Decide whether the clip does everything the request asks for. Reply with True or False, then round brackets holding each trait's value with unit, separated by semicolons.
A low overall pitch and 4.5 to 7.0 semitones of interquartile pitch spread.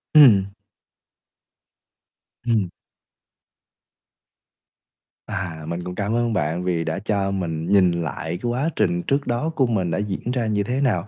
True (100 Hz; 5.4 semitones)